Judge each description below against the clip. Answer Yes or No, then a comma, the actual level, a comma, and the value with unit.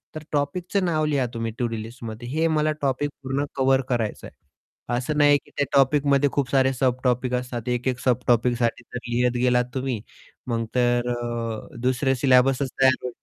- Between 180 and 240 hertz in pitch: No, low, 125 Hz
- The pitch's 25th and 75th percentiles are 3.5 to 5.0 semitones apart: No, narrow, 2.4 semitones